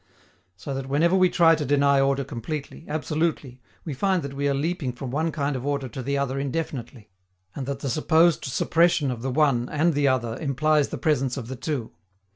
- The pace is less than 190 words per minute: No, fast, 205 wpm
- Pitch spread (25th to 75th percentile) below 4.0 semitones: Yes, average, 2.9 semitones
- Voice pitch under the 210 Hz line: Yes, medium, 140 Hz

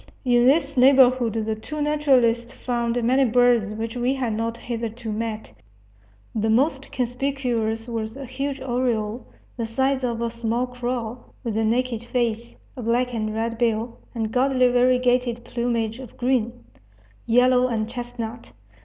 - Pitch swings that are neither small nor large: No, narrow, 1.9 semitones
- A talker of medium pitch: No, high, 240 Hz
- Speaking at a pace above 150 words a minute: No, average, 145 wpm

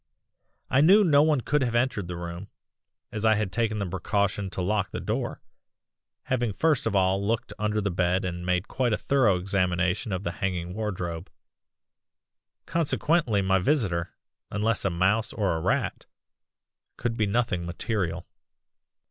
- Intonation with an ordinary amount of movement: Yes, average, 4.2 semitones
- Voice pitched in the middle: No, low, 100 Hz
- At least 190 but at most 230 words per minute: No, average, 155 wpm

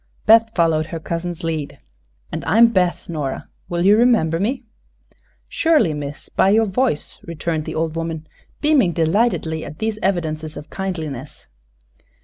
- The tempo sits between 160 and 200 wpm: No, average, 145 wpm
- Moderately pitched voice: Yes, medium, 170 Hz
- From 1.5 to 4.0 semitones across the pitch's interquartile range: No, average, 5.2 semitones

